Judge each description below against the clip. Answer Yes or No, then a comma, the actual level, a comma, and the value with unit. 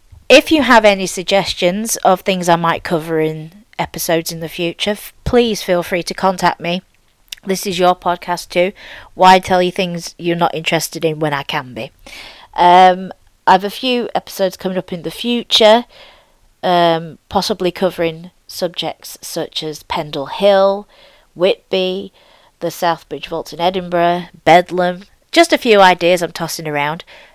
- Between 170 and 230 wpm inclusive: No, average, 155 wpm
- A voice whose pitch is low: No, medium, 180 Hz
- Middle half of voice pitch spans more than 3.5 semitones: No, average, 2.7 semitones